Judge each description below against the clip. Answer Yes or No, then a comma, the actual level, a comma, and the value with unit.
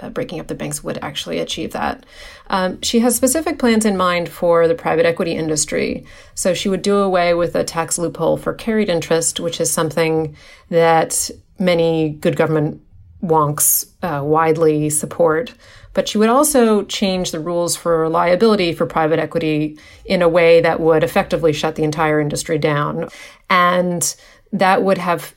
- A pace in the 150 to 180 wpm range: Yes, average, 170 wpm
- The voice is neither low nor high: Yes, medium, 170 Hz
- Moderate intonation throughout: Yes, average, 3.0 semitones